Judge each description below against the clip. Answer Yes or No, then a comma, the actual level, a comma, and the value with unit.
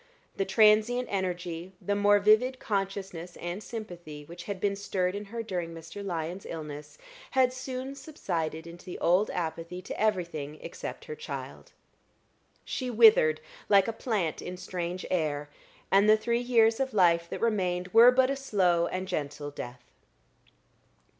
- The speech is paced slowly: No, average, 155 wpm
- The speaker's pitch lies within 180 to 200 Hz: Yes, high, 190 Hz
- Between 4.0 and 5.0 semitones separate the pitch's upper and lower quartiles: Yes, average, 4.4 semitones